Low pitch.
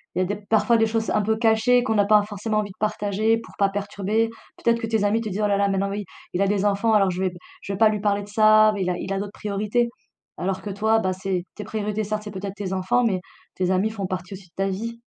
No: high, 205 Hz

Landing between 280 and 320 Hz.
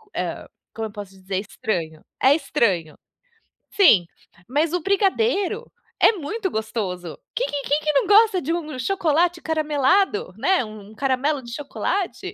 Yes: very high, 290 Hz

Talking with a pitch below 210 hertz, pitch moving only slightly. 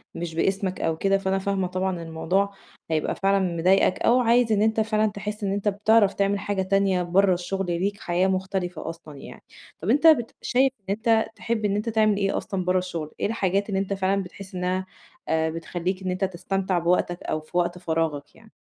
Yes: high, 190 Hz; narrow, 2.3 semitones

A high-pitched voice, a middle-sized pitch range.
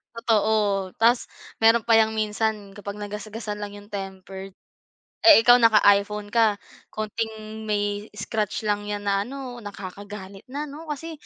No: high, 210 Hz; narrow, 1.8 semitones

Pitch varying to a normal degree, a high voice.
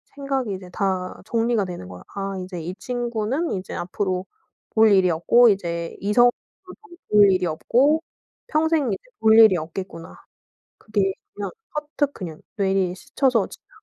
Yes: average, 4.8 semitones; high, 200 Hz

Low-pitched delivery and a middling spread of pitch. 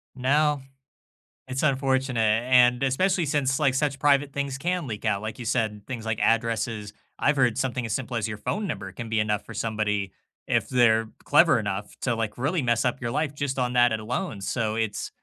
Yes: low, 125 Hz; average, 3.8 semitones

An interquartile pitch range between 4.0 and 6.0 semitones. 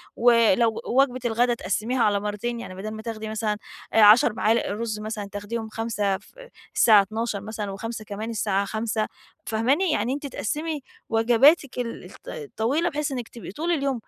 No: average, 2.7 semitones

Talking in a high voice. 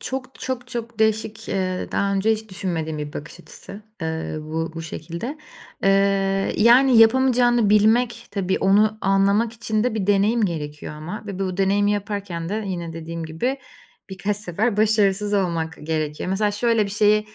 Yes: high, 200 Hz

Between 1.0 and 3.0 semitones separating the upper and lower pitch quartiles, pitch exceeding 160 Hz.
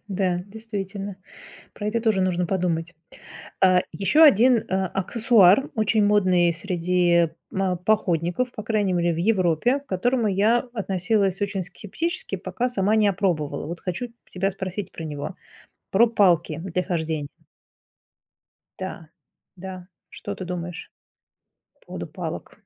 No: average, 3.4 semitones; high, 190 Hz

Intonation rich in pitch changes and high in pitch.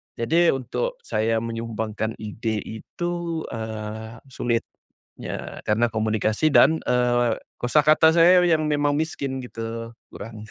No: wide, 5.8 semitones; low, 115 Hz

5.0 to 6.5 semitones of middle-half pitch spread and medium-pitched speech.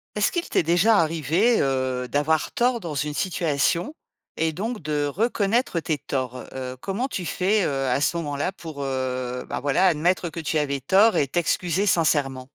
Yes: average, 5.3 semitones; medium, 160 Hz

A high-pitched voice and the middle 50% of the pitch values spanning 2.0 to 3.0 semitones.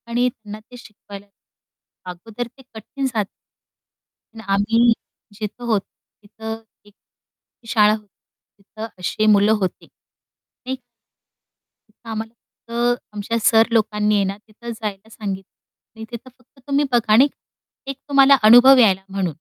Yes: high, 220 Hz; narrow, 2.5 semitones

